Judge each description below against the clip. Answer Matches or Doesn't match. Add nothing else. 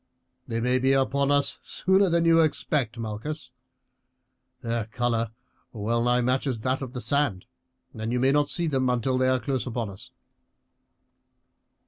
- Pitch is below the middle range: Matches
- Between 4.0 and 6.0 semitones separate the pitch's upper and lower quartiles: Doesn't match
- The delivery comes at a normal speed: Matches